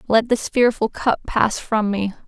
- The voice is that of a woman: Yes, female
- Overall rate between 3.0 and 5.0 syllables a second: Yes, 4.2 syllables/s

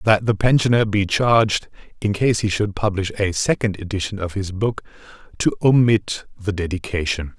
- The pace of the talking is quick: No, average, 165 wpm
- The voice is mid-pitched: No, low, 100 Hz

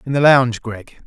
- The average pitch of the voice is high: No, low, 125 Hz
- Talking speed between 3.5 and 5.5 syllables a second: No, 5.8 syllables/s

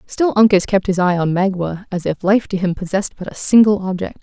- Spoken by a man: No, female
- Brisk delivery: Yes, fast, 240 wpm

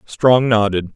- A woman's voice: No, male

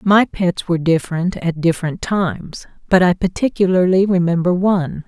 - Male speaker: No, female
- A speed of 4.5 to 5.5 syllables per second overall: Yes, 5.3 syllables/s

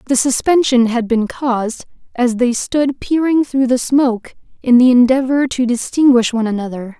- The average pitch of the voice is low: No, very high, 250 Hz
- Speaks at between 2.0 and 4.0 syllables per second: No, 4.9 syllables/s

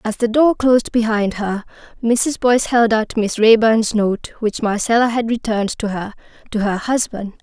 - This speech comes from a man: No, female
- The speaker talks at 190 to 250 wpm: No, average, 180 wpm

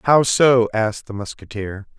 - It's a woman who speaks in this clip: No, male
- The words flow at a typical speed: Yes, average, 150 wpm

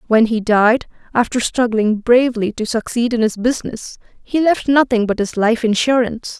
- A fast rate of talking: No, average, 170 wpm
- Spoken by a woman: Yes, female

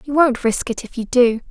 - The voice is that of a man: No, female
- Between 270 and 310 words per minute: Yes, fast, 280 wpm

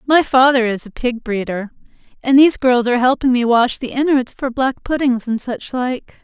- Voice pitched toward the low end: No, very high, 250 Hz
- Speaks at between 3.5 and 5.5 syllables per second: Yes, 5.2 syllables/s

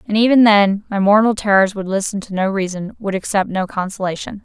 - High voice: Yes, high, 200 Hz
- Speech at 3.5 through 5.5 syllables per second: No, 5.7 syllables/s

